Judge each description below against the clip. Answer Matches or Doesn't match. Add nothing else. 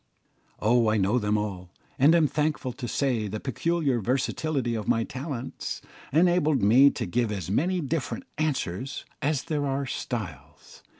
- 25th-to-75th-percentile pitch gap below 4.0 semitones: Doesn't match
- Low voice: Matches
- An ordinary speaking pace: Matches